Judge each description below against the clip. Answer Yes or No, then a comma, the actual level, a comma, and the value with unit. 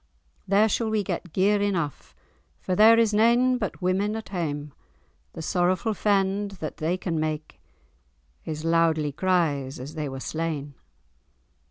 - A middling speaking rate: Yes, average, 145 wpm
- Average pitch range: Yes, average, 4.8 semitones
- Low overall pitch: No, medium, 180 Hz